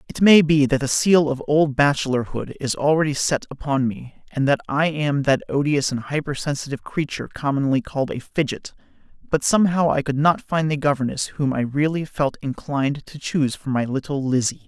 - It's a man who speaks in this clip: Yes, male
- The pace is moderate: Yes, average, 190 wpm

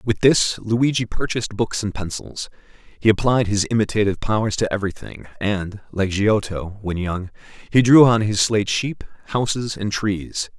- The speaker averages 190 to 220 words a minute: No, average, 160 wpm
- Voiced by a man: Yes, male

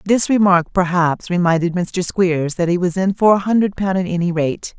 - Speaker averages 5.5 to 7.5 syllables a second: No, 5.0 syllables/s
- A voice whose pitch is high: No, medium, 180 Hz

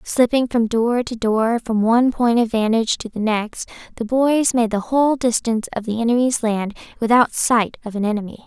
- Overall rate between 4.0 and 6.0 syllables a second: Yes, 5.3 syllables/s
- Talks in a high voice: Yes, high, 230 Hz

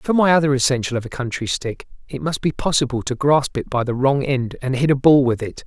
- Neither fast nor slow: No, fast, 275 wpm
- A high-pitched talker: No, low, 135 Hz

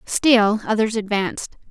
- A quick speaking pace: No, slow, 105 wpm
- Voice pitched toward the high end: Yes, high, 215 Hz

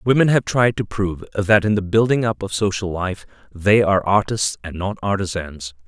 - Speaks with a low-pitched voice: Yes, low, 100 Hz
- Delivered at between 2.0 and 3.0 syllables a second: No, 5.2 syllables/s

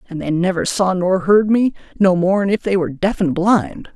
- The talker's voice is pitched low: No, high, 190 Hz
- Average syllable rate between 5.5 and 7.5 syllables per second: No, 5.1 syllables/s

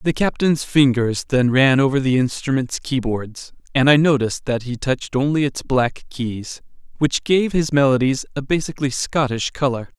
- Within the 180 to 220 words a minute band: No, average, 160 wpm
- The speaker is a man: Yes, male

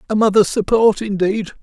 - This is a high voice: Yes, high, 205 Hz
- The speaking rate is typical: Yes, average, 150 wpm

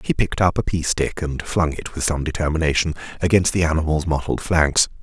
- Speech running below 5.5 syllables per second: No, 5.7 syllables/s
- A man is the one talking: Yes, male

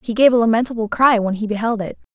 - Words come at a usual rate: No, fast, 250 wpm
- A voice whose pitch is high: Yes, high, 225 Hz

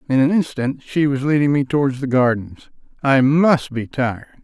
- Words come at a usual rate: Yes, average, 190 wpm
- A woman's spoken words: No, male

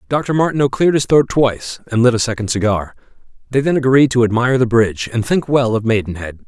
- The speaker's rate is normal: No, fast, 215 wpm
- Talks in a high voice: No, low, 120 Hz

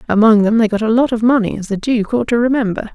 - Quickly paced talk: Yes, fast, 265 wpm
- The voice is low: No, high, 225 Hz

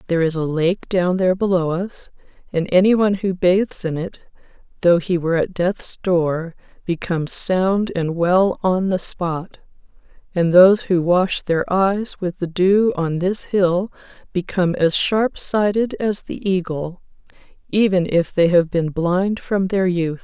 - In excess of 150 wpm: Yes, average, 165 wpm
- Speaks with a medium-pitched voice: Yes, medium, 180 Hz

